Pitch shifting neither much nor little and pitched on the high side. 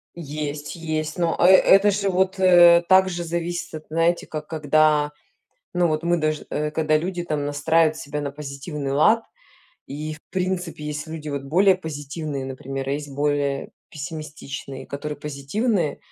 No: average, 3.0 semitones; medium, 155 Hz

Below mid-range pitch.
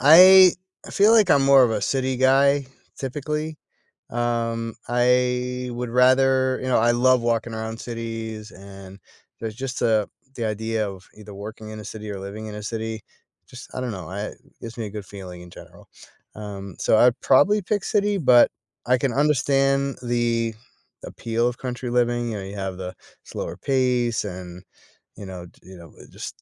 Yes: low, 120 Hz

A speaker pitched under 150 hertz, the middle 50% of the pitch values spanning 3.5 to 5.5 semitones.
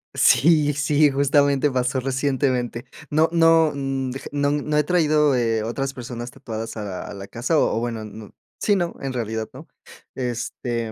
Yes: low, 135 Hz; average, 3.9 semitones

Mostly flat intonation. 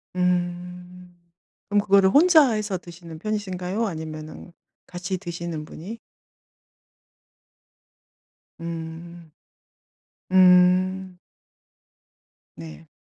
Yes: narrow, 2.0 semitones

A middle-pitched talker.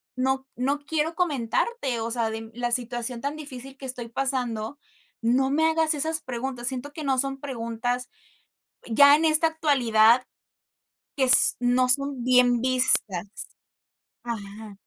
No: very high, 255 Hz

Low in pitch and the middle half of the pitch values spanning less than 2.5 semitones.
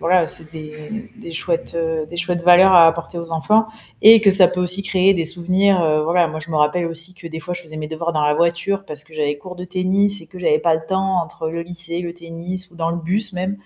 No: medium, 170 Hz; narrow, 2.1 semitones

